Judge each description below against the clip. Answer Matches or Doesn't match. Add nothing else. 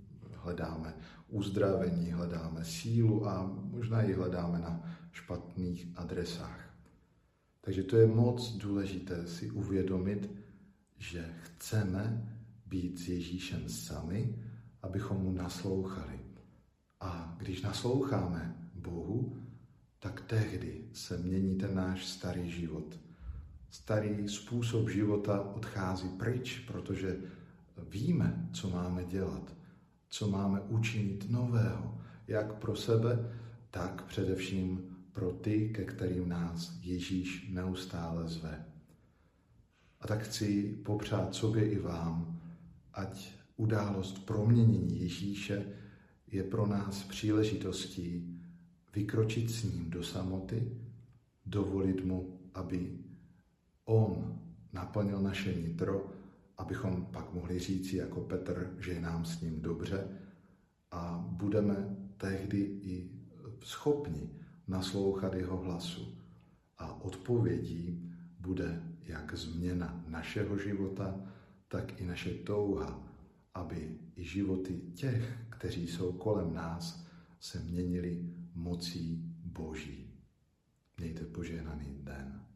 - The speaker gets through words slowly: Matches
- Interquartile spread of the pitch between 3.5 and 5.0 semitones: Doesn't match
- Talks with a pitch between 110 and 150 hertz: Doesn't match